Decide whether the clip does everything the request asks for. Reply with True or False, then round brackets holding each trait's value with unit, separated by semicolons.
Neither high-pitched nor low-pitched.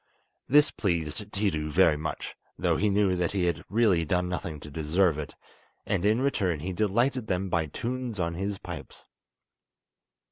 False (90 Hz)